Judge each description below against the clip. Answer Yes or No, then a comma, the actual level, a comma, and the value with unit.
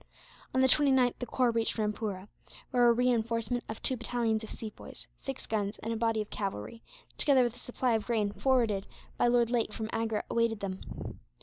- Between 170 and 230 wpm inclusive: Yes, average, 190 wpm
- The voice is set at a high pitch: Yes, high, 230 Hz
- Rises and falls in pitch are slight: Yes, narrow, 2.1 semitones